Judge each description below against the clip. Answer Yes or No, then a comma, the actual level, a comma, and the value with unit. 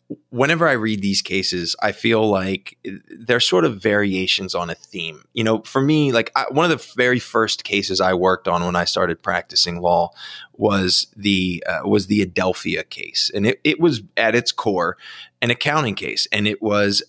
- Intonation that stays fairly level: No, average, 4.0 semitones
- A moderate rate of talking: Yes, average, 195 wpm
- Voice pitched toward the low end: Yes, low, 105 Hz